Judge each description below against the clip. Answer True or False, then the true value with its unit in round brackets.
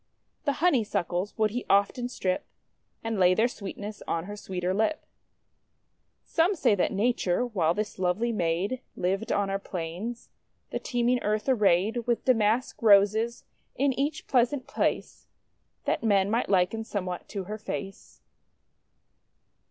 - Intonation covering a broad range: False (4.0 semitones)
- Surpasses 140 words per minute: False (135 wpm)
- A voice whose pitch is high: True (215 Hz)